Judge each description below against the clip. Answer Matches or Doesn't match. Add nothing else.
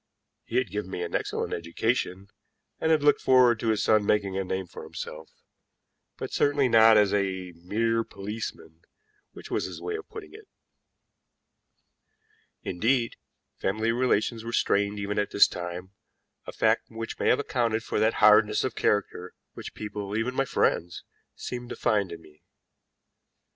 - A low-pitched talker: Matches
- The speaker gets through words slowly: Doesn't match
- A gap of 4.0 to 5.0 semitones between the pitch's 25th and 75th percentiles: Doesn't match